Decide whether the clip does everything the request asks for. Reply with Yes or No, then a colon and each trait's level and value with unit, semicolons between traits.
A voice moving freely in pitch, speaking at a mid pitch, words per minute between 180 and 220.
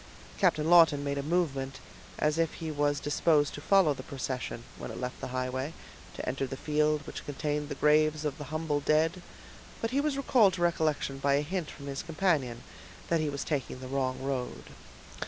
No: average, 2.8 semitones; medium, 150 Hz; average, 195 wpm